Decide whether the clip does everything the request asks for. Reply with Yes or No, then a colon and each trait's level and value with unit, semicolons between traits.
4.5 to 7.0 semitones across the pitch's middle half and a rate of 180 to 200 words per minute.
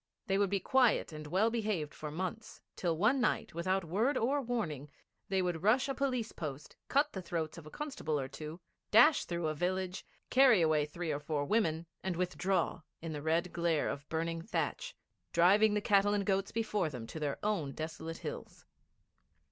Yes: average, 5.2 semitones; average, 190 wpm